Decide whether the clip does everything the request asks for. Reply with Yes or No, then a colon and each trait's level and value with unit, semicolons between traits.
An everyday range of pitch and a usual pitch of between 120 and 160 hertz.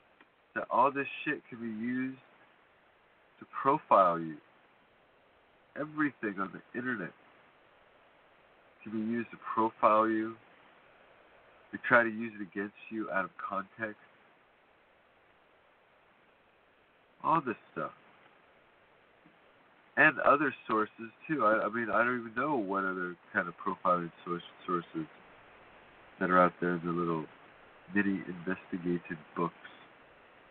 No: average, 4.3 semitones; low, 100 Hz